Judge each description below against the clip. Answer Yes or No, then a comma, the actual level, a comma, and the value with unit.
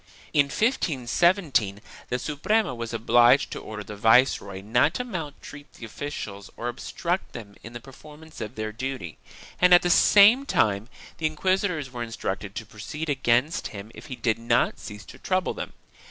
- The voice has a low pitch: Yes, low, 125 Hz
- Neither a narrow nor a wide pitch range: No, wide, 6.4 semitones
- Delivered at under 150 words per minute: No, average, 170 wpm